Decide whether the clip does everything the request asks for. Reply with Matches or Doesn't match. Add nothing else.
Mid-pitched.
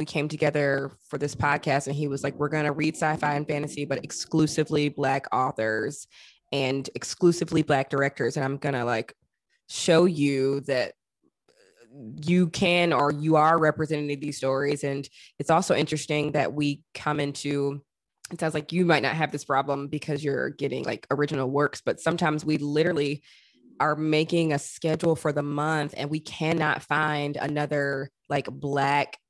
Matches